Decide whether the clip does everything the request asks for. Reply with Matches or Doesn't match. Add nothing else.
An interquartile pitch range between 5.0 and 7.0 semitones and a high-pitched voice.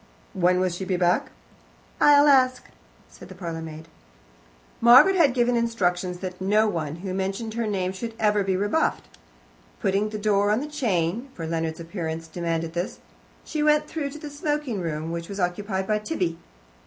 Matches